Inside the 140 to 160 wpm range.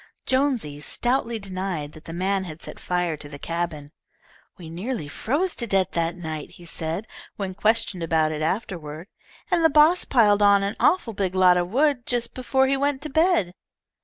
No: average, 185 wpm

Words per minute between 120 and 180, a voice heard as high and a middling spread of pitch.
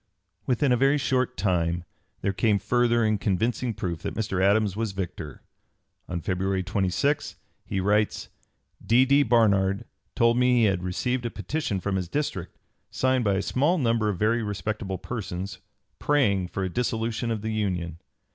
No: average, 165 wpm; low, 105 Hz; average, 4.2 semitones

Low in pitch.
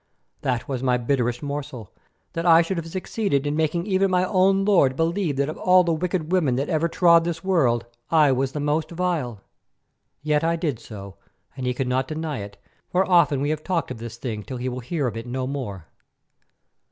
No: medium, 150 Hz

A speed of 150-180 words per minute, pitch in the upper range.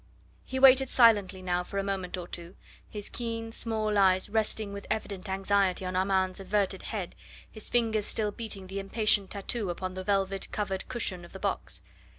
Yes: average, 175 wpm; high, 200 Hz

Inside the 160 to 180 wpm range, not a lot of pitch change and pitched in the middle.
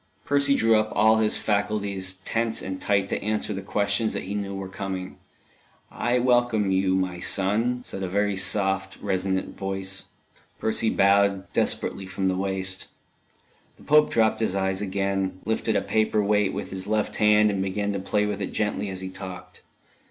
No: average, 175 wpm; narrow, 2.1 semitones; low, 100 Hz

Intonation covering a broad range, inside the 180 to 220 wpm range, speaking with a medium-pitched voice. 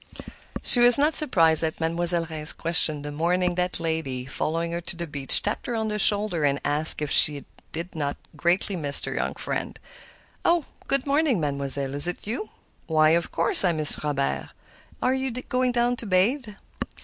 Yes: wide, 6.3 semitones; average, 185 wpm; medium, 170 Hz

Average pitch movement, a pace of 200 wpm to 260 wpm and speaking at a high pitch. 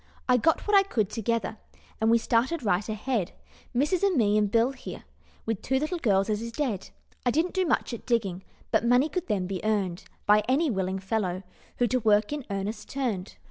Yes: average, 4.6 semitones; fast, 205 wpm; high, 230 Hz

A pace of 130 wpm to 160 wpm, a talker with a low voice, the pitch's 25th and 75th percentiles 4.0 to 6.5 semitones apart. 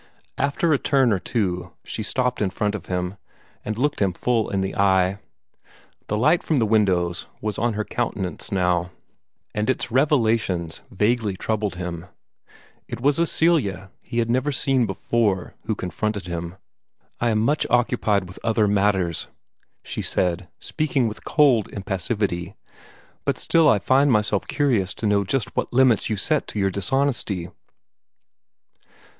Yes: average, 155 wpm; low, 105 Hz; average, 4.5 semitones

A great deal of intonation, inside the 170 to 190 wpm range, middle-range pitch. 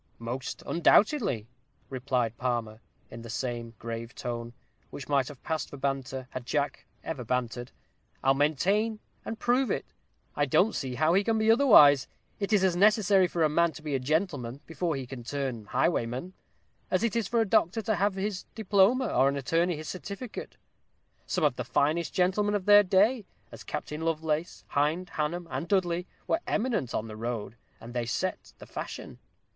Yes: wide, 7.3 semitones; average, 180 wpm; medium, 155 Hz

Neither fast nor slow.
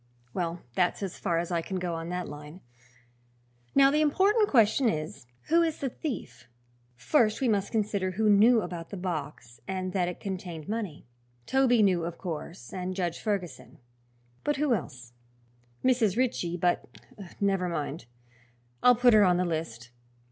Yes: average, 160 wpm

